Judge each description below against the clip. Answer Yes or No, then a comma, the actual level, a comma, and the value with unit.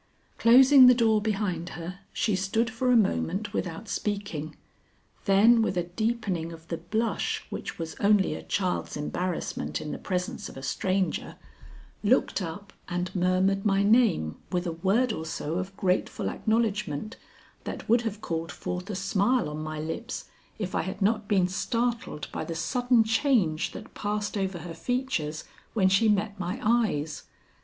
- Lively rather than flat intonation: No, average, 4.3 semitones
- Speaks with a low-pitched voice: No, high, 195 Hz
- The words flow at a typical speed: Yes, average, 165 wpm